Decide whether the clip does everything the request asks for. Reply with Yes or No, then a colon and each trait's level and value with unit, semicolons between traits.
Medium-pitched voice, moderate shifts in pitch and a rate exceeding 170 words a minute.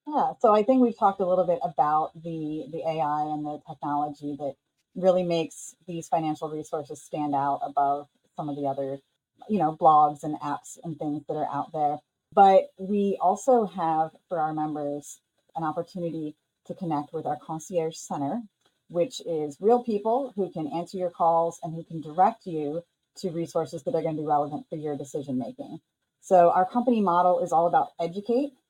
Yes: medium, 165 Hz; average, 3.5 semitones; average, 185 wpm